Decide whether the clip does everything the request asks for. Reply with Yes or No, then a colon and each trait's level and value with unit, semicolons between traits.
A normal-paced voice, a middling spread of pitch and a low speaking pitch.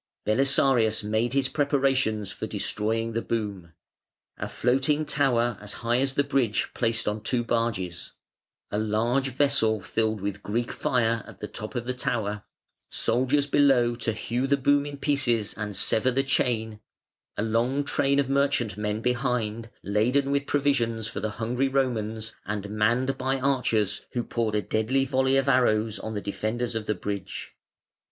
Yes: average, 160 wpm; average, 3.8 semitones; low, 120 Hz